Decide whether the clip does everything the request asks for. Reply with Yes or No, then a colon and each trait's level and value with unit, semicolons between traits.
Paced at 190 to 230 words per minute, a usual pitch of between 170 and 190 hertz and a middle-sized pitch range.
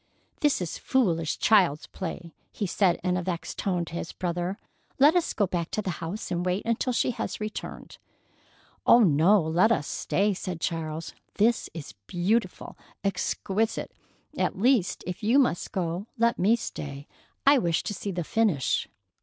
No: average, 165 wpm; medium, 185 Hz; average, 4.5 semitones